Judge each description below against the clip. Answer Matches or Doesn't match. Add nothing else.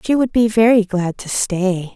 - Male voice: Doesn't match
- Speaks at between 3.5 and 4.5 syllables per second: Matches